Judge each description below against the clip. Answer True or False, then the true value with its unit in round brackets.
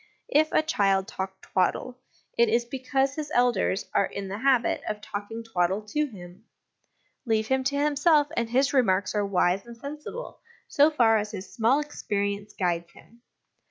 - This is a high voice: True (225 Hz)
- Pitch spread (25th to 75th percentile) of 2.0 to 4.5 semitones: False (5.4 semitones)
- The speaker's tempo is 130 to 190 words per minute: True (165 wpm)